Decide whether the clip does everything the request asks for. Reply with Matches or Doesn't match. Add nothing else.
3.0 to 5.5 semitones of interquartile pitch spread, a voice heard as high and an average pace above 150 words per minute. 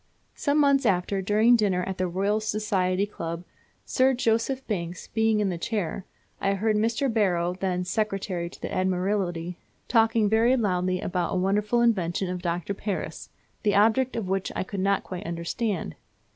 Matches